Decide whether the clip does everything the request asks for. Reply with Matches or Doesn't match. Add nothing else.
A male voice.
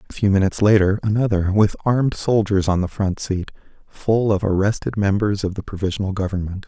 Matches